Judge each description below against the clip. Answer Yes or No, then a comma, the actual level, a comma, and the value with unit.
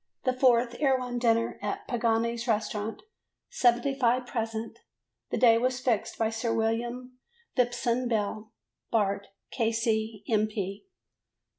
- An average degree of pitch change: No, narrow, 1.8 semitones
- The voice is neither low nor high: No, high, 230 Hz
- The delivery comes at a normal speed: No, slow, 110 wpm